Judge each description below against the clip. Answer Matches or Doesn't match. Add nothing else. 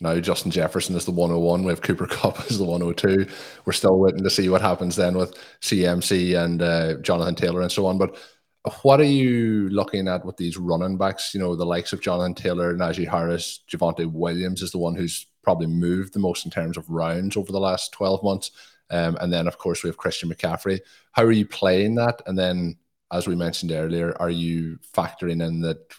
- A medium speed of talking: Doesn't match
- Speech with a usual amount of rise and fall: Doesn't match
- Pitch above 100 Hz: Doesn't match